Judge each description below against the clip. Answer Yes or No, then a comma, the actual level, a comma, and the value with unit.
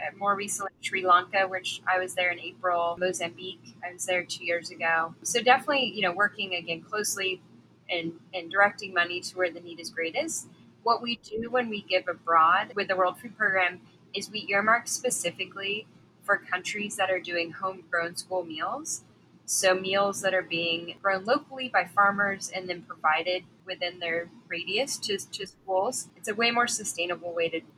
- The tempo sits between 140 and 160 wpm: No, average, 180 wpm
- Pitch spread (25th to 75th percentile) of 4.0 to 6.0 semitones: No, narrow, 2.6 semitones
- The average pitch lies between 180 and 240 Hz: Yes, medium, 185 Hz